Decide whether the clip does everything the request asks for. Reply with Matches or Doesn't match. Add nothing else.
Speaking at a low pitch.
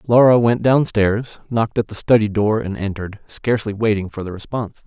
Matches